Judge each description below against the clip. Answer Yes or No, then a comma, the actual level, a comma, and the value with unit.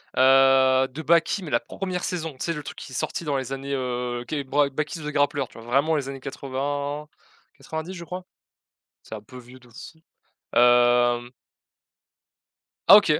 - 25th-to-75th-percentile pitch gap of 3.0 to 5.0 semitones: Yes, average, 3.3 semitones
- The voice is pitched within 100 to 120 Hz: No, low, 135 Hz